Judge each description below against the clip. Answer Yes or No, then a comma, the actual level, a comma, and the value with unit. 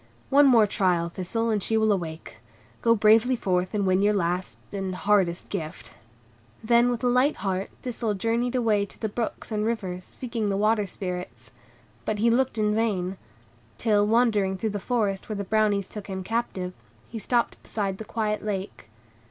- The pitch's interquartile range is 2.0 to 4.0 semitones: Yes, average, 3.1 semitones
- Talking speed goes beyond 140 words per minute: Yes, average, 175 wpm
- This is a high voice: Yes, high, 210 Hz